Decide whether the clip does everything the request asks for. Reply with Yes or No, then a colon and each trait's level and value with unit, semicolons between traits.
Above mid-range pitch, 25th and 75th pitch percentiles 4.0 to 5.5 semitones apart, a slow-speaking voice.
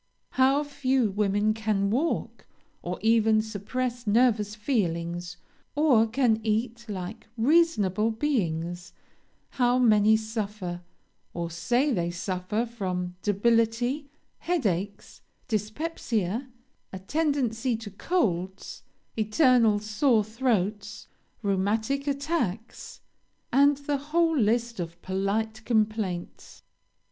Yes: high, 220 Hz; average, 4.3 semitones; slow, 95 wpm